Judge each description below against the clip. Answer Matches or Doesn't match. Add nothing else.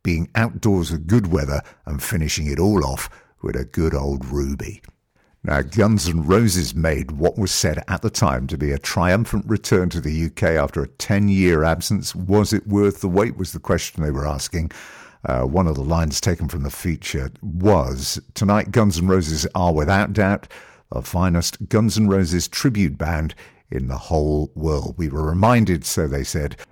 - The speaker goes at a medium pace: Matches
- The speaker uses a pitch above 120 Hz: Doesn't match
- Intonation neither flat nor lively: Matches